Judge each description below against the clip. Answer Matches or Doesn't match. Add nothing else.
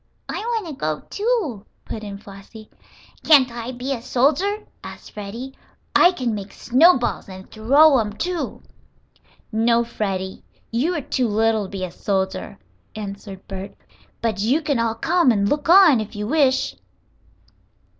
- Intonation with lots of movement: Matches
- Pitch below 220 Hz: Doesn't match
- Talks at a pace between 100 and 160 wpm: Matches